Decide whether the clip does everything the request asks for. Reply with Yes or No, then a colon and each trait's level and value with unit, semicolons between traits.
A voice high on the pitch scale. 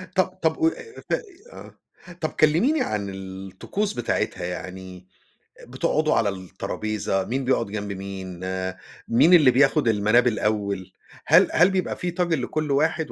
No: low, 115 Hz